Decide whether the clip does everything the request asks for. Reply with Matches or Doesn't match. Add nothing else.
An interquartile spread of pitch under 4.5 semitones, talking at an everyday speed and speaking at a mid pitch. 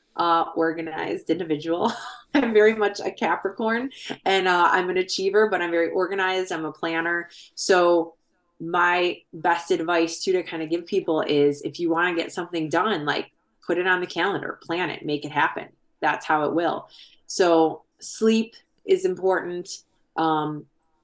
Matches